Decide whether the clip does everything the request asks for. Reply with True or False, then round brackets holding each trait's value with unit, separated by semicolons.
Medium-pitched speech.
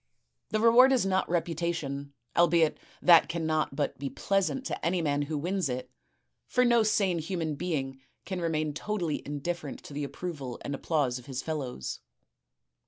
True (160 Hz)